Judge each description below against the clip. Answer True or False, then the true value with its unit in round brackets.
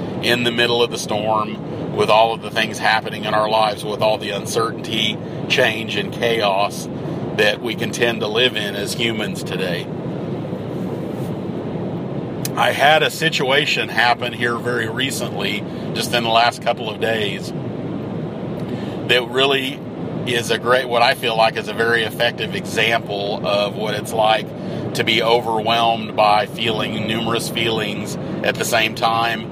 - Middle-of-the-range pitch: False (115 Hz)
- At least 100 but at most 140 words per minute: False (155 wpm)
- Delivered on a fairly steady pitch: True (1.6 semitones)